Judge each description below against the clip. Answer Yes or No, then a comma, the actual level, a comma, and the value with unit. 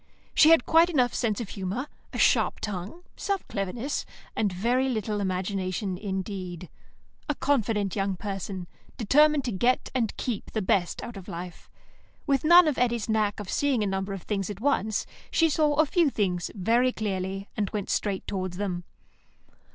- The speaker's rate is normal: Yes, average, 170 wpm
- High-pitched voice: Yes, high, 210 Hz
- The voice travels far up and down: No, average, 4.9 semitones